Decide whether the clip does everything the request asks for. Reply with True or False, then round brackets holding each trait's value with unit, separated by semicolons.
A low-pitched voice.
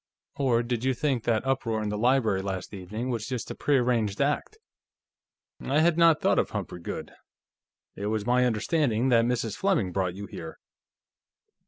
True (120 Hz)